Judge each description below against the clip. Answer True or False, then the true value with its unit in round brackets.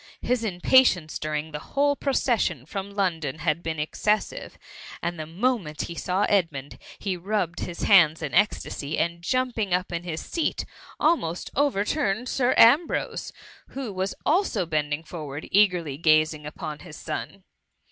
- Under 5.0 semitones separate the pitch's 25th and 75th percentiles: False (5.4 semitones)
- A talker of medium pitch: True (180 Hz)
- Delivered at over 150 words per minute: False (145 wpm)